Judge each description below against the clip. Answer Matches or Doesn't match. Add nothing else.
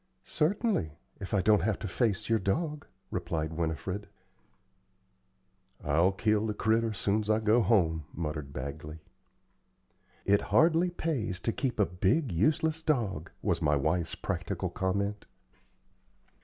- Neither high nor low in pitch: Doesn't match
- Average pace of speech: Doesn't match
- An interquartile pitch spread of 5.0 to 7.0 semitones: Matches